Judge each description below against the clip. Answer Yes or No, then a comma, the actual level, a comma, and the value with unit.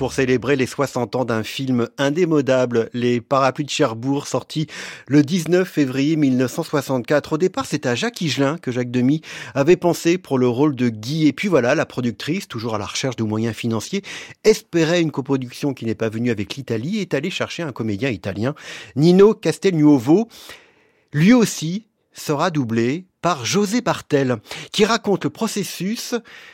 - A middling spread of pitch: No, wide, 5.7 semitones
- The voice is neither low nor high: Yes, medium, 145 Hz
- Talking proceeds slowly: No, average, 165 wpm